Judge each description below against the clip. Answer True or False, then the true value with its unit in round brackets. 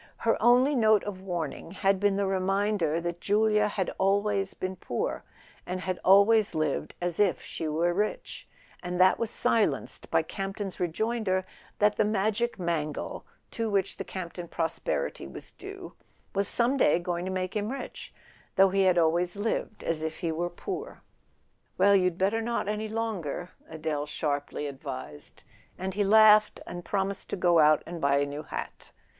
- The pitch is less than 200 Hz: True (190 Hz)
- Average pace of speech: True (170 wpm)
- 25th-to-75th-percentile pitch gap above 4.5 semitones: False (3.5 semitones)